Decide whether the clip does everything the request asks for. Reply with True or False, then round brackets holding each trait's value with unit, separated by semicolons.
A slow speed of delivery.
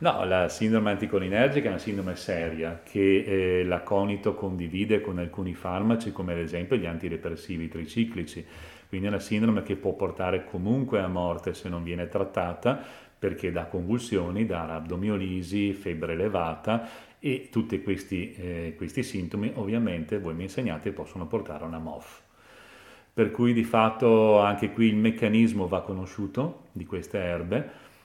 False (150 wpm)